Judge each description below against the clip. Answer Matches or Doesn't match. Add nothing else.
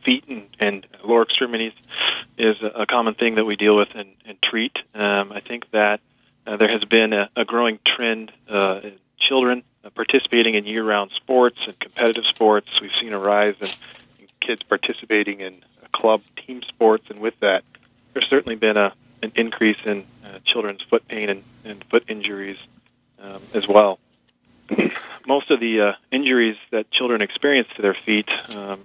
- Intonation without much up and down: Matches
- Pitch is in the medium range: Doesn't match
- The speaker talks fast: Doesn't match